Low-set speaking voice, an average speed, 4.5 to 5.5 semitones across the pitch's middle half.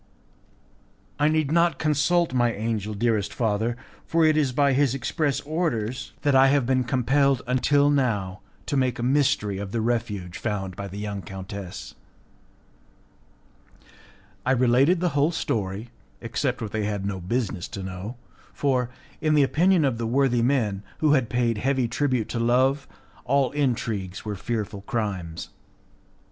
Yes: low, 120 Hz; average, 155 wpm; average, 5.0 semitones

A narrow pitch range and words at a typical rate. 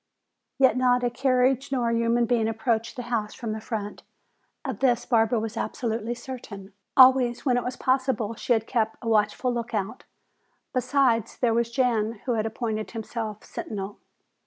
Yes: narrow, 2.3 semitones; average, 165 wpm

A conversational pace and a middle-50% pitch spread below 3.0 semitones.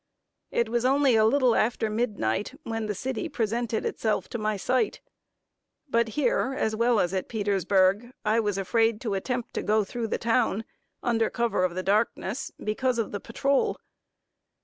Yes: average, 170 wpm; narrow, 2.6 semitones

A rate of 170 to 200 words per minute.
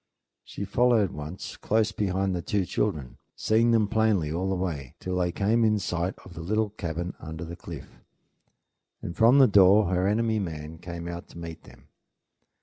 Yes: average, 180 wpm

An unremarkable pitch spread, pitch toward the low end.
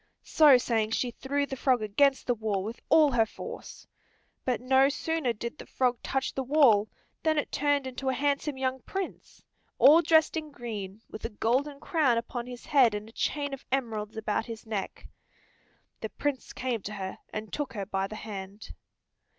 No: average, 4.4 semitones; very high, 250 Hz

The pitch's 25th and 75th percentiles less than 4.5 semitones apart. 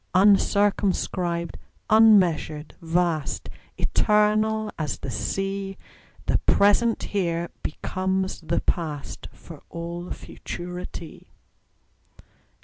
Yes: average, 3.2 semitones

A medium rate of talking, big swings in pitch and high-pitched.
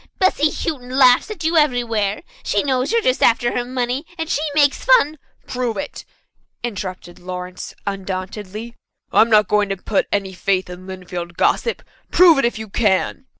Yes: average, 170 wpm; wide, 6.0 semitones; high, 235 Hz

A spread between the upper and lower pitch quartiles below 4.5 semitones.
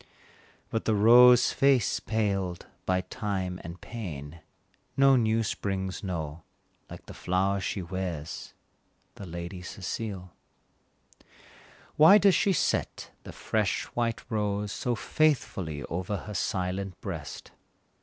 Yes: average, 3.9 semitones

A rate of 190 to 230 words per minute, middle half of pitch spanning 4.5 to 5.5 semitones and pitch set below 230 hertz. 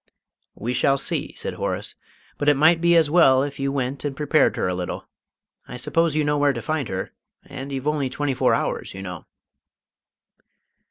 No: average, 195 wpm; narrow, 2.5 semitones; medium, 140 Hz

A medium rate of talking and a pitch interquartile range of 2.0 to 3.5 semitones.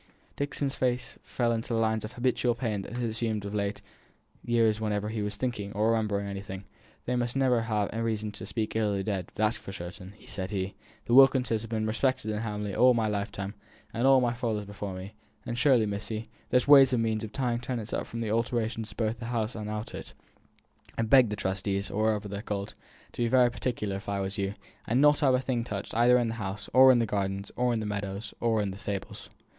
No: fast, 230 wpm; average, 2.8 semitones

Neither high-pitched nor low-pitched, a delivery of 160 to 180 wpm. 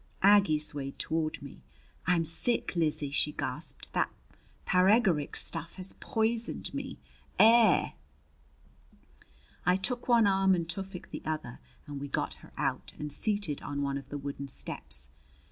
No: medium, 165 Hz; average, 145 wpm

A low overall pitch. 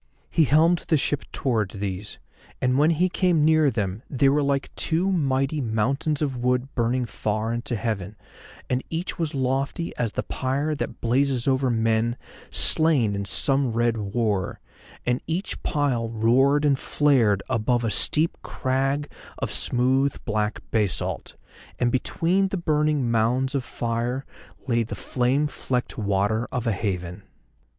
Yes: low, 130 Hz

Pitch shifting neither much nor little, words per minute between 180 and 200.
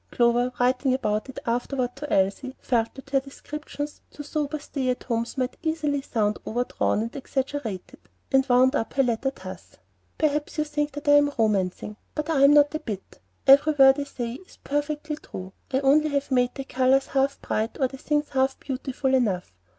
Yes: average, 3.1 semitones; average, 190 wpm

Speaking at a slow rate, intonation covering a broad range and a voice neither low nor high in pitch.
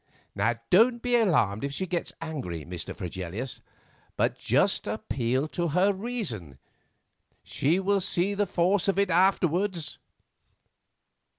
Yes: slow, 120 wpm; wide, 7.7 semitones; medium, 175 Hz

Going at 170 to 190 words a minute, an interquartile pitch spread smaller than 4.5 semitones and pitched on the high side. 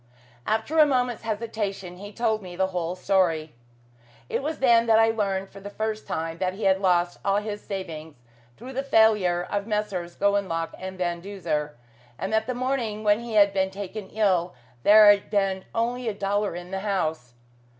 Yes: average, 185 wpm; average, 3.1 semitones; high, 200 Hz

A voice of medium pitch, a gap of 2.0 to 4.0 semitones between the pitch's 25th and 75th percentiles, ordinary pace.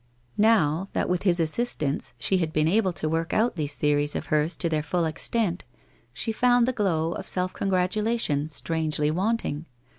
No: medium, 170 Hz; average, 4.4 semitones; average, 175 wpm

